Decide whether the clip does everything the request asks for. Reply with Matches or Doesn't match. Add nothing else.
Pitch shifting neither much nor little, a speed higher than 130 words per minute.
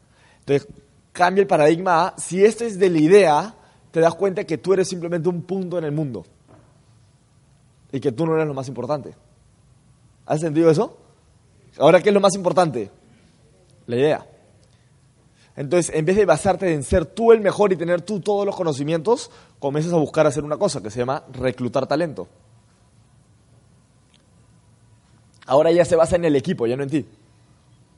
Doesn't match